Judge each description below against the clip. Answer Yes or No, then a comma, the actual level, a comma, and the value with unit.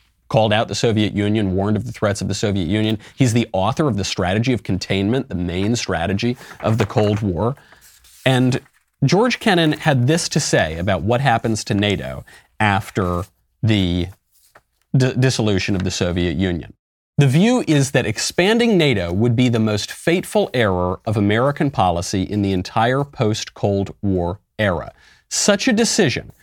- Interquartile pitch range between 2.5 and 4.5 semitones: No, wide, 5.4 semitones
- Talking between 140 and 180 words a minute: Yes, average, 165 wpm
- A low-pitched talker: Yes, low, 110 Hz